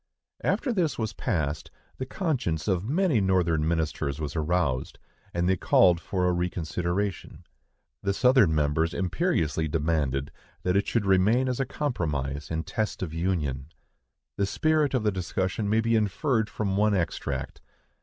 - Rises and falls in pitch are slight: No, wide, 5.6 semitones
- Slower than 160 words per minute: Yes, average, 150 wpm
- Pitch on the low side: Yes, very low, 95 Hz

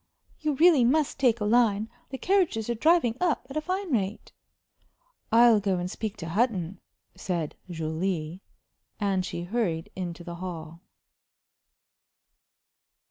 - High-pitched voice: Yes, high, 210 Hz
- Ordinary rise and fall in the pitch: No, wide, 6.1 semitones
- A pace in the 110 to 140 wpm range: Yes, slow, 135 wpm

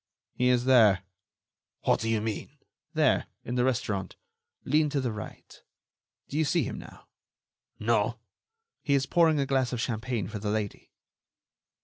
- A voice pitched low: Yes, low, 125 Hz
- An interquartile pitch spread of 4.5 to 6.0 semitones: No, average, 4.0 semitones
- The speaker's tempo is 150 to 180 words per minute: Yes, average, 155 wpm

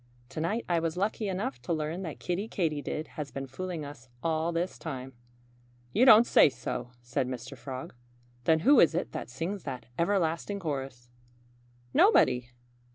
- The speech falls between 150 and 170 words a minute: Yes, average, 160 wpm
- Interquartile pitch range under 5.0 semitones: No, average, 5.3 semitones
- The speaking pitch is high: No, medium, 160 Hz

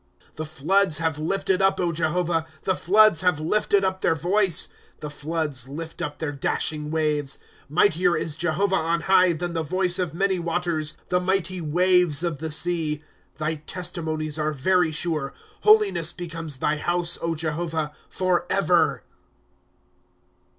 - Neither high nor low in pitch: Yes, medium, 165 Hz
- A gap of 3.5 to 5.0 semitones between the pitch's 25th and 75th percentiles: No, average, 2.8 semitones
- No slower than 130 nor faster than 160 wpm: Yes, average, 150 wpm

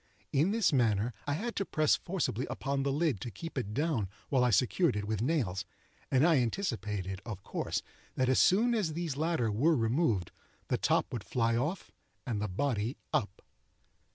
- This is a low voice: Yes, low, 130 Hz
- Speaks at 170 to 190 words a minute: Yes, average, 180 wpm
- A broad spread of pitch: Yes, wide, 6.8 semitones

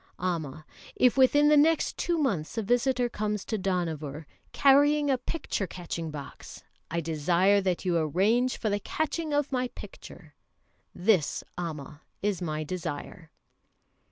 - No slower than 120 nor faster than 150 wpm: Yes, average, 140 wpm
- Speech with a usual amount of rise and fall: No, wide, 7.7 semitones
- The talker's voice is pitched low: No, high, 195 Hz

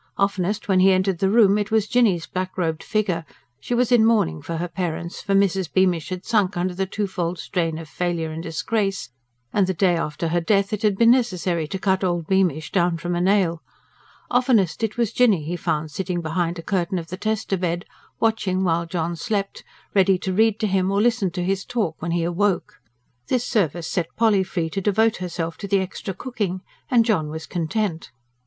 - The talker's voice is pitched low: No, medium, 185 Hz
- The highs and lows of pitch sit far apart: No, average, 3.2 semitones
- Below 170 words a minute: No, fast, 205 wpm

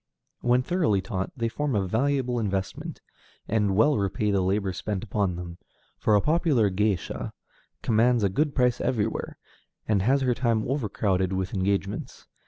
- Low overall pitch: Yes, low, 105 Hz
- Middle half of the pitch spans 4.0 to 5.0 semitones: Yes, average, 4.3 semitones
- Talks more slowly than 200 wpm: Yes, average, 155 wpm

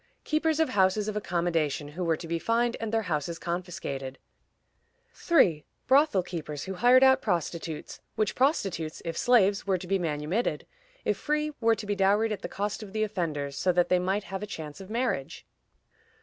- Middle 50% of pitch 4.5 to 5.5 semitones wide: Yes, average, 5.1 semitones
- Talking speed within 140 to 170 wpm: No, average, 185 wpm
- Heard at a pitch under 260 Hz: Yes, high, 190 Hz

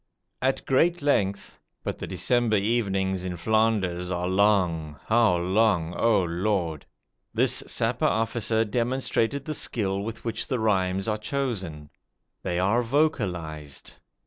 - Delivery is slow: Yes, slow, 125 wpm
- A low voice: Yes, low, 105 Hz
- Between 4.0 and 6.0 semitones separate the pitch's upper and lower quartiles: Yes, average, 4.4 semitones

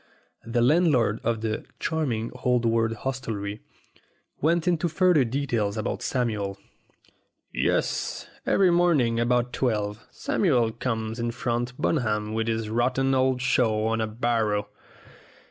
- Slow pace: Yes, slow, 125 wpm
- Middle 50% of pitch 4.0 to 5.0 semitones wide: No, average, 3.0 semitones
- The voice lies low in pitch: Yes, low, 120 Hz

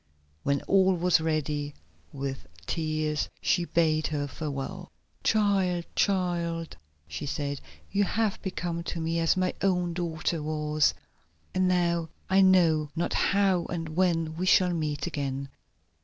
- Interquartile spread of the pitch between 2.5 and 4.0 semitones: Yes, average, 3.0 semitones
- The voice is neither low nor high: Yes, medium, 165 Hz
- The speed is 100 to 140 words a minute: Yes, slow, 135 wpm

